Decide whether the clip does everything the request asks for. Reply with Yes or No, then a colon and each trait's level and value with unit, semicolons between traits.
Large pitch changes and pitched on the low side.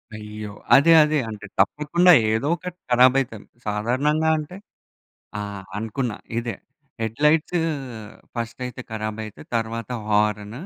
Yes: wide, 5.7 semitones; low, 120 Hz